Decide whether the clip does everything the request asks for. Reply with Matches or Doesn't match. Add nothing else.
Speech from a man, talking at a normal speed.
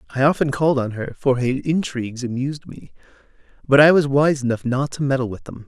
Doesn't match